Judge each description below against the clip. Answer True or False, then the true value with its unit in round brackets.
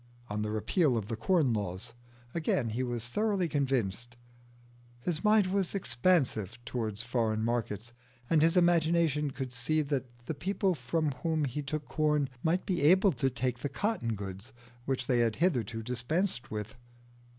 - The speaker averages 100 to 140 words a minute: False (160 wpm)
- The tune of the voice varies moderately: False (6.0 semitones)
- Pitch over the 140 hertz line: False (135 Hz)